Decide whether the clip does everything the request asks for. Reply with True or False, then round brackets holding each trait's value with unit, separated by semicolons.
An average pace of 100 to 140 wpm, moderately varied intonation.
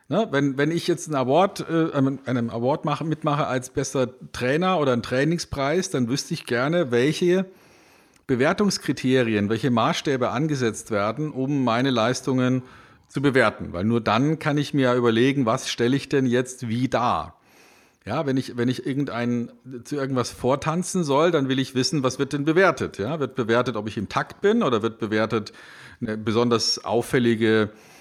False (165 wpm; 3.9 semitones)